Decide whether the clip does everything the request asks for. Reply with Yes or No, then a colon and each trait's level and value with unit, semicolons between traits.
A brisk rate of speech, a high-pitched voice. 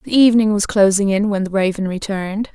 Yes: fast, 210 wpm; high, 200 Hz